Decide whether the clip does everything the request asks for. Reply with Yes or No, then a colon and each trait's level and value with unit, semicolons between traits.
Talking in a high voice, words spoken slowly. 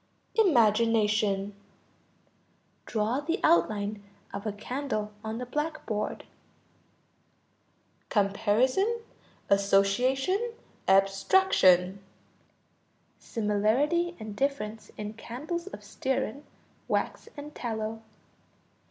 Yes: high, 225 Hz; slow, 75 wpm